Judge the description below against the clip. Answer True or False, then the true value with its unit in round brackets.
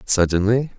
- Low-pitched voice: True (105 Hz)